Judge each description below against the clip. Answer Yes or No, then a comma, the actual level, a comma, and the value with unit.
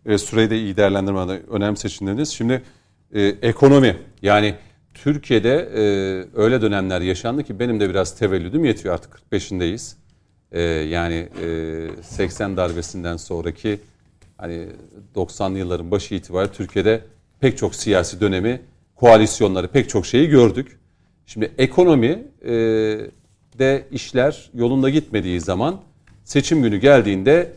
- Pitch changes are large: No, average, 4.3 semitones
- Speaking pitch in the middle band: No, low, 105 Hz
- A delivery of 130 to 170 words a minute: No, average, 120 wpm